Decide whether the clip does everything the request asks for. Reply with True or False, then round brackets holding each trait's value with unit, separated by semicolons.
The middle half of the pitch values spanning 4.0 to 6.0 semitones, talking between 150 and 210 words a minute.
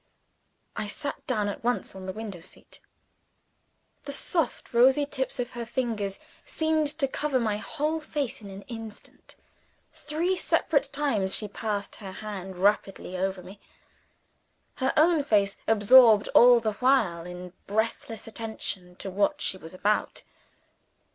False (5.0 semitones; 140 wpm)